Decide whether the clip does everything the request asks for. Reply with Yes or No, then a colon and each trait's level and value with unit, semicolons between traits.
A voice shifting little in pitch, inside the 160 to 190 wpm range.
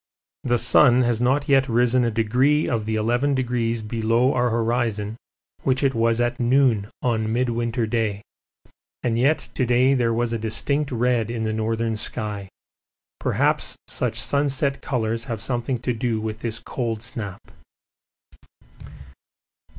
No: narrow, 2.1 semitones; average, 145 wpm